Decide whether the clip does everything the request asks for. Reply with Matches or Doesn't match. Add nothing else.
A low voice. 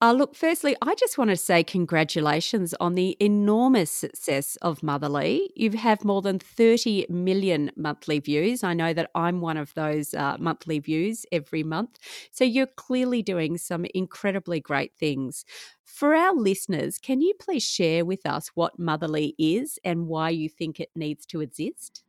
Doesn't match